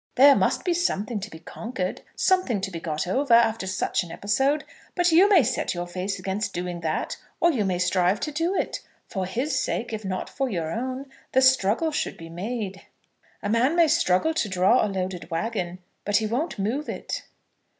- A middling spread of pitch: No, wide, 6.6 semitones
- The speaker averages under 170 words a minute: No, average, 200 wpm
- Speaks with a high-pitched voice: Yes, high, 210 Hz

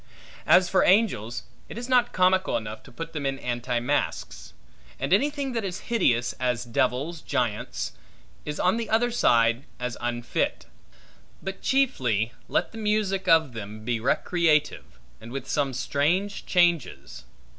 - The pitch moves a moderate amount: No, wide, 8.2 semitones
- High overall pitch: No, medium, 150 Hz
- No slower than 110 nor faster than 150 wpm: Yes, average, 145 wpm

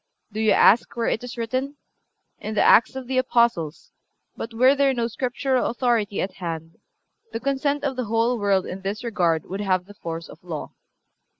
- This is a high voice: Yes, high, 230 Hz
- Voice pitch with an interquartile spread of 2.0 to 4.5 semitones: No, average, 5.0 semitones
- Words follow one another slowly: No, average, 190 wpm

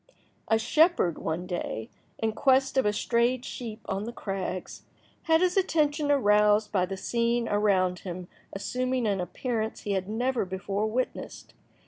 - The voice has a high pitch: Yes, high, 220 Hz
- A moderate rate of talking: Yes, average, 150 wpm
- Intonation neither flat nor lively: Yes, average, 4.8 semitones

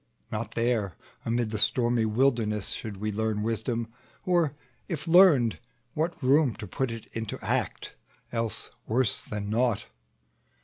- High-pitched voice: No, low, 115 Hz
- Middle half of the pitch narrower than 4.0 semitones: Yes, average, 3.3 semitones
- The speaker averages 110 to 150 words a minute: Yes, slow, 135 wpm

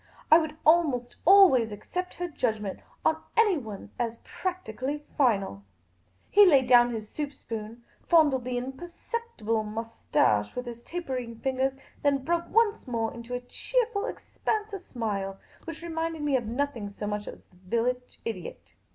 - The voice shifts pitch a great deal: Yes, wide, 6.5 semitones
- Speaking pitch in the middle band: No, very high, 255 Hz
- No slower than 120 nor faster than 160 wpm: Yes, average, 155 wpm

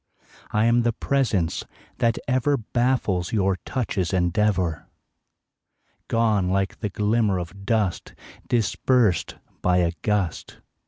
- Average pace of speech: No, slow, 110 wpm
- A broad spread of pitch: No, average, 4.2 semitones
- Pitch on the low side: Yes, low, 105 Hz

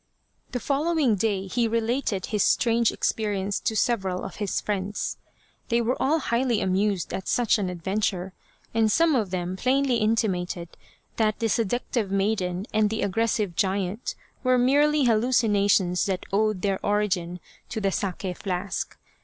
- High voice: Yes, high, 210 Hz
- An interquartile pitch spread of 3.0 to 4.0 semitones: Yes, average, 3.6 semitones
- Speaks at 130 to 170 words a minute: Yes, average, 150 wpm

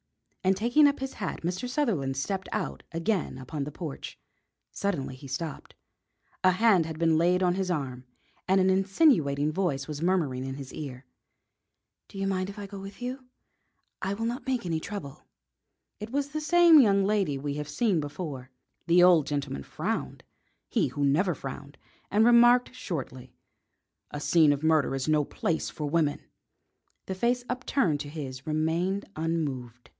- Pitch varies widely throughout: Yes, wide, 5.7 semitones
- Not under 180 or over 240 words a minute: No, average, 170 wpm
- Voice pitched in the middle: Yes, medium, 170 Hz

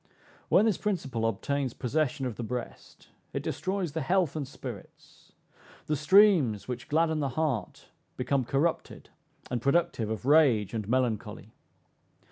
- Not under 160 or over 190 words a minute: No, slow, 135 wpm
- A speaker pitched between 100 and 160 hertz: Yes, low, 135 Hz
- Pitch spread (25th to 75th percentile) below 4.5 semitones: No, average, 4.9 semitones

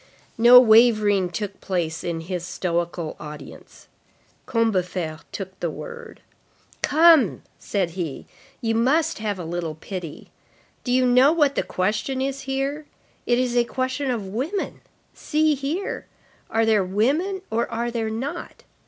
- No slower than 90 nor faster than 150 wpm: Yes, average, 140 wpm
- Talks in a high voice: Yes, high, 225 Hz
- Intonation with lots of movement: Yes, wide, 6.7 semitones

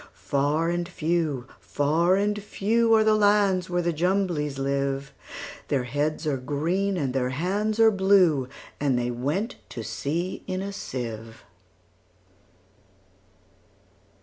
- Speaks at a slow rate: Yes, slow, 115 wpm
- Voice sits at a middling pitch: Yes, medium, 165 Hz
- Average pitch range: No, wide, 6.0 semitones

